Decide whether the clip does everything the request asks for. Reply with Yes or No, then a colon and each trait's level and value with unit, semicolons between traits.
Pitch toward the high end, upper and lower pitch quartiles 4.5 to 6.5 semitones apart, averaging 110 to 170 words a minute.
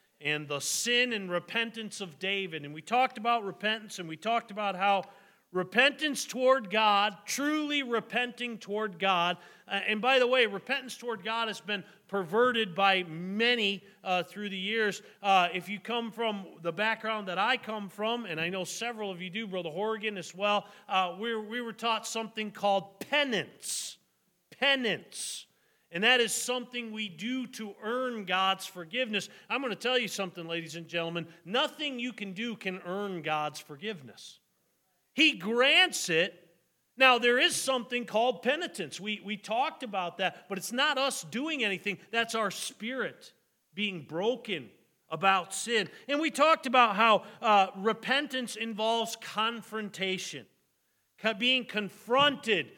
No: high, 215 Hz; average, 4.1 semitones; average, 155 wpm